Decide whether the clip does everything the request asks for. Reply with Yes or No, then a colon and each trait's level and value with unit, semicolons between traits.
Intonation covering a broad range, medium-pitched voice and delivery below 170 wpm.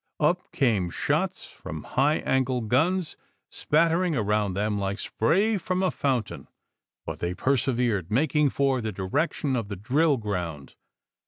No: wide, 6.9 semitones; low, 125 Hz; average, 140 wpm